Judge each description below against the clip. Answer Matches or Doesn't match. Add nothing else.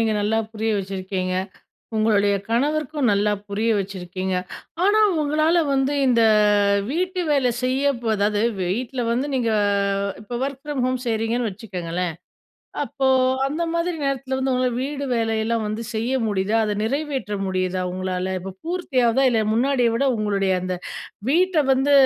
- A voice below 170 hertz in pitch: Doesn't match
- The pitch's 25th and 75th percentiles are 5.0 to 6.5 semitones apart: Matches